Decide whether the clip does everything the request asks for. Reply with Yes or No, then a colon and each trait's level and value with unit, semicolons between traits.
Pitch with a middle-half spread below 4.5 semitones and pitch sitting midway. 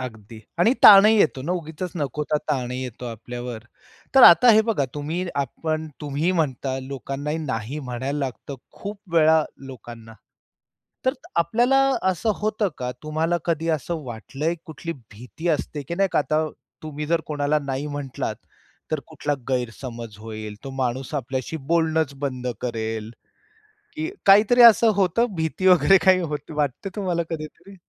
No: average, 5.0 semitones; medium, 150 Hz